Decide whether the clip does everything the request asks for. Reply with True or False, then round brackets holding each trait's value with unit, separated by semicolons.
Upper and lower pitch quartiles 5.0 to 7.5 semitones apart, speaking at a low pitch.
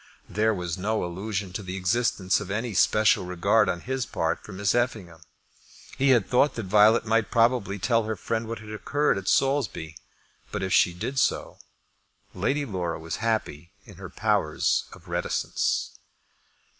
False (3.9 semitones; 105 Hz)